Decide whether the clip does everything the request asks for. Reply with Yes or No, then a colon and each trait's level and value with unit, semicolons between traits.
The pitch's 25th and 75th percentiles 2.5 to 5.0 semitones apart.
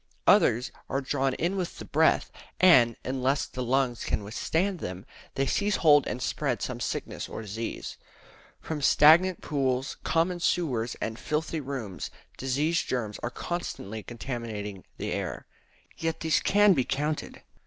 No: wide, 5.4 semitones